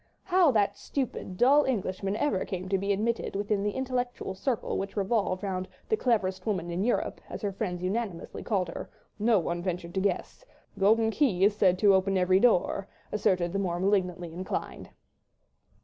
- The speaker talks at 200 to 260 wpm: No, average, 175 wpm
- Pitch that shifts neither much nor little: Yes, average, 3.2 semitones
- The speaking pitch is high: Yes, high, 195 Hz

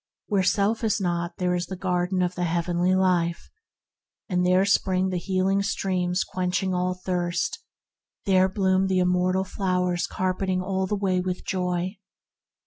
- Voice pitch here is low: No, medium, 185 Hz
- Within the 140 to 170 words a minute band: Yes, average, 155 wpm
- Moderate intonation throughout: No, narrow, 1.0 semitones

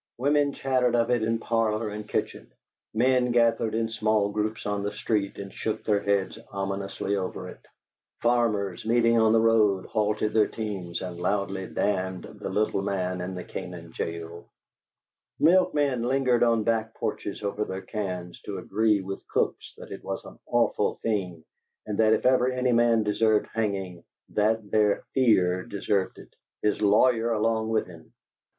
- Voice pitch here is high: No, low, 105 Hz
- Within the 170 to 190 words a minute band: No, average, 160 wpm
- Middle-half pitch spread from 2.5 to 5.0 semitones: Yes, average, 2.8 semitones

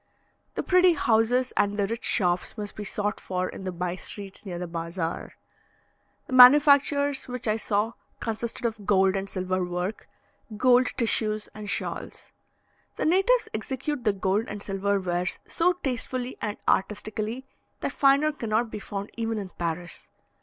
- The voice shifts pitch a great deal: No, average, 4.6 semitones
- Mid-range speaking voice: No, high, 215 Hz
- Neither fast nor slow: Yes, average, 155 wpm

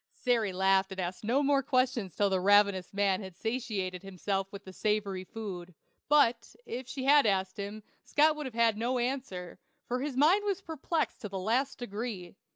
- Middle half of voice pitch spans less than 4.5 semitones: No, average, 5.1 semitones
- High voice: Yes, high, 215 Hz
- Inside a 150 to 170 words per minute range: No, average, 185 wpm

